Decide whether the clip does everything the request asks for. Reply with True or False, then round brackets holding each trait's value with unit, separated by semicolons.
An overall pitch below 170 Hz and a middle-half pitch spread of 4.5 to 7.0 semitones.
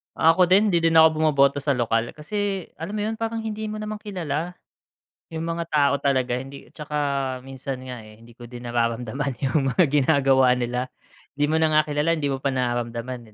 True (140 Hz; 4.9 semitones)